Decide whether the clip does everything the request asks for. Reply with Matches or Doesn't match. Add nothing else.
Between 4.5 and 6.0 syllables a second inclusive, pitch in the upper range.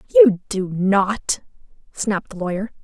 Matches